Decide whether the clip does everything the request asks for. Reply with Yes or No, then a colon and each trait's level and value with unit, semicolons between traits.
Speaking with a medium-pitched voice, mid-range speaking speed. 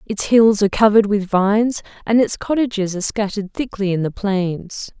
No: high, 205 Hz; average, 180 wpm